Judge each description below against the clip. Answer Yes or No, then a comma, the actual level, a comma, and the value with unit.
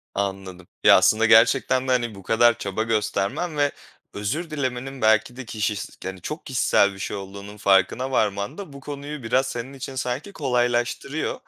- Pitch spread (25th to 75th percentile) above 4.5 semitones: Yes, average, 4.9 semitones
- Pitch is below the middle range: Yes, low, 120 Hz